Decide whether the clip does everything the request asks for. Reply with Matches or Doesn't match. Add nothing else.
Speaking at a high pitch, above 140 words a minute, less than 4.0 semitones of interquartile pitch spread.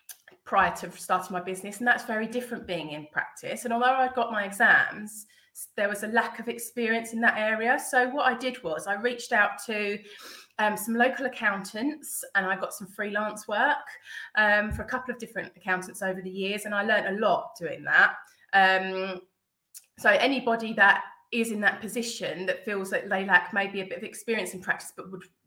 Matches